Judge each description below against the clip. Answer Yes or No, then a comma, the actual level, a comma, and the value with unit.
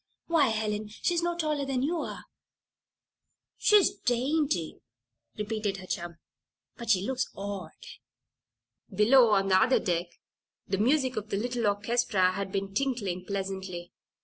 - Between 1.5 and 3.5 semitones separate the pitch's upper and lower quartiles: No, average, 5.2 semitones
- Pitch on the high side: Yes, high, 215 Hz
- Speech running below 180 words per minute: Yes, slow, 135 wpm